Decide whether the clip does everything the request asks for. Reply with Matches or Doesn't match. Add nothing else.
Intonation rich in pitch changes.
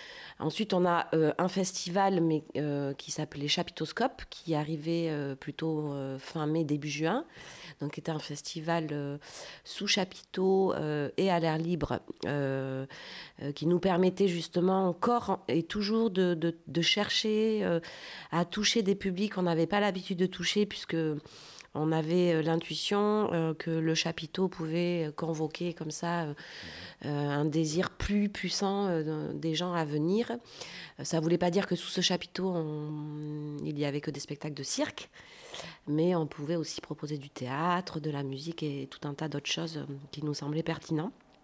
Doesn't match